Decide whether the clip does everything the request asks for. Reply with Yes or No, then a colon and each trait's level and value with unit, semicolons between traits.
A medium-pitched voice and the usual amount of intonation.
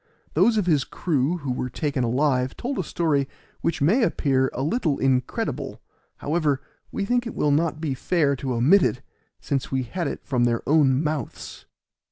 Yes: medium, 145 Hz; average, 4.3 semitones